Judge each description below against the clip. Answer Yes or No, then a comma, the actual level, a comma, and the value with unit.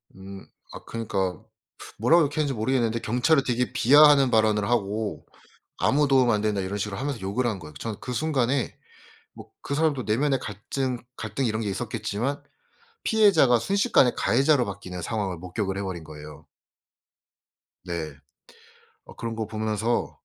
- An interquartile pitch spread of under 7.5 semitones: Yes, average, 5.1 semitones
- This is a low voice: Yes, low, 115 Hz